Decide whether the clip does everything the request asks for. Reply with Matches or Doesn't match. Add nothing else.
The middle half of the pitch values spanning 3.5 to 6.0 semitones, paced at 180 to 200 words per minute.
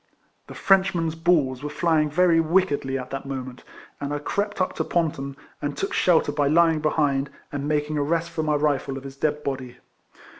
Doesn't match